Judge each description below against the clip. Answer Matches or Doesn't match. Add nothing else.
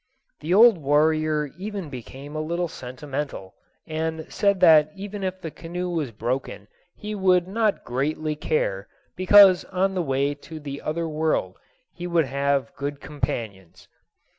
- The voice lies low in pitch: Doesn't match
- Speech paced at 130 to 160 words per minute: Matches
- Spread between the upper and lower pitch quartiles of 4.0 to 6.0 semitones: Matches